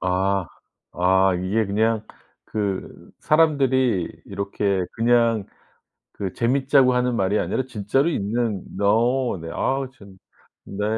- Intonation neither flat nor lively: Yes, average, 4.4 semitones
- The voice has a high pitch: No, low, 110 Hz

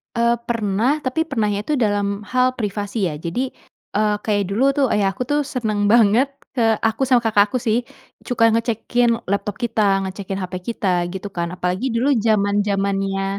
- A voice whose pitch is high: Yes, high, 215 Hz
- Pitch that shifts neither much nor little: Yes, average, 3.2 semitones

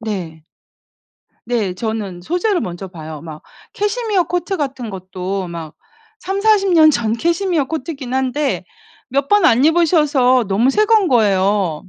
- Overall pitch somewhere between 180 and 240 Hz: No, very high, 255 Hz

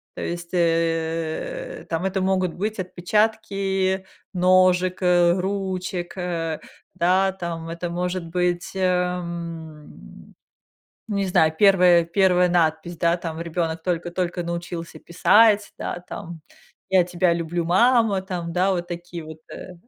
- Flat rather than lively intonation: Yes, narrow, 1.8 semitones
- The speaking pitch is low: No, medium, 175 Hz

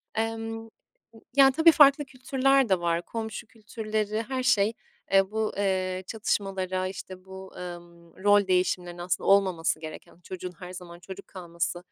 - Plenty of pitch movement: No, average, 3.7 semitones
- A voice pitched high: Yes, high, 195 Hz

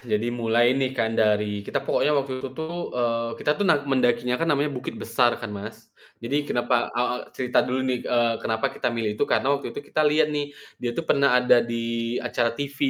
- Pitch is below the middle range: Yes, low, 125 Hz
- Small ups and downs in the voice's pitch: No, average, 3.1 semitones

